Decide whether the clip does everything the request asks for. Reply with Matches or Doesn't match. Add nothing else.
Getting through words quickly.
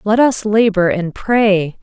Doesn't match